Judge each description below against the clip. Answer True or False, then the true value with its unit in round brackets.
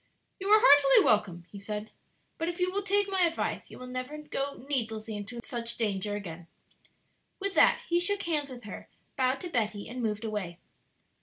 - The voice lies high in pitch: True (250 Hz)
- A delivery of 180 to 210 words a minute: True (185 wpm)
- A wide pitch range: True (7.9 semitones)